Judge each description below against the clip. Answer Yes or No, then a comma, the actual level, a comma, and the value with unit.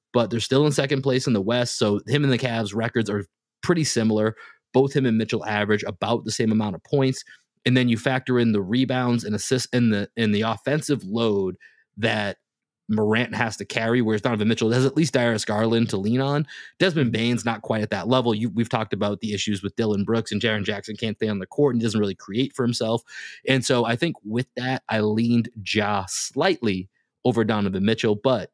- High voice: No, low, 115 Hz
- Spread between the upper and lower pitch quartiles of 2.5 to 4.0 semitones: Yes, average, 3.0 semitones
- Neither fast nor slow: No, fast, 220 wpm